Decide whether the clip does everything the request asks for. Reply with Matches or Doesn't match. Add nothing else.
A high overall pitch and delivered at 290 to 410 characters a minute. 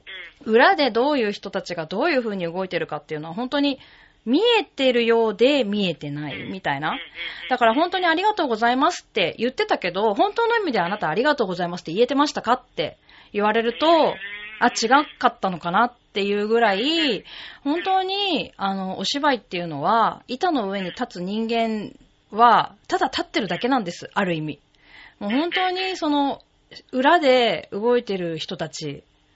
Matches